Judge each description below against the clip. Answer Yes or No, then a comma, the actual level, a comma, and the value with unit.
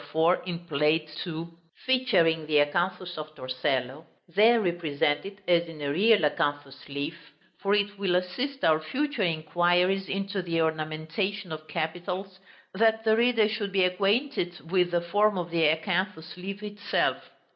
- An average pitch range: Yes, average, 4.1 semitones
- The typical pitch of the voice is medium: Yes, medium, 175 Hz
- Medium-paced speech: No, slow, 130 wpm